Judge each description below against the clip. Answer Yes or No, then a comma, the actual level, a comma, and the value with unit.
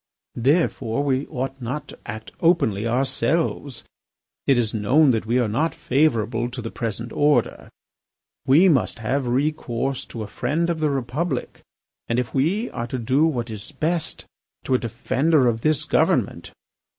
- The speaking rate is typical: Yes, average, 160 wpm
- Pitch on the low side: Yes, low, 130 Hz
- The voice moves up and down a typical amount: Yes, average, 4.3 semitones